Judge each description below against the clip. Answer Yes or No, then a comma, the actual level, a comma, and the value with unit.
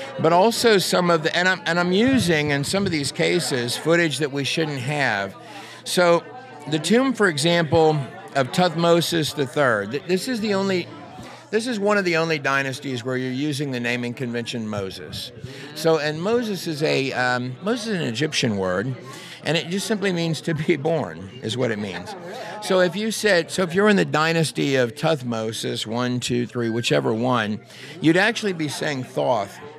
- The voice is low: No, medium, 155 Hz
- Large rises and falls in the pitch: Yes, wide, 5.9 semitones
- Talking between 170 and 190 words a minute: Yes, average, 185 wpm